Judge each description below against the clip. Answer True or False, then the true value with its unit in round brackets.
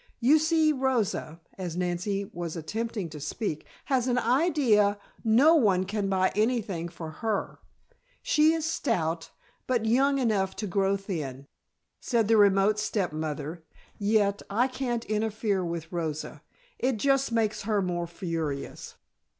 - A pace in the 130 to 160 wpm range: True (140 wpm)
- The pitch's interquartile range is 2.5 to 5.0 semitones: False (5.6 semitones)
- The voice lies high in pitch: True (205 Hz)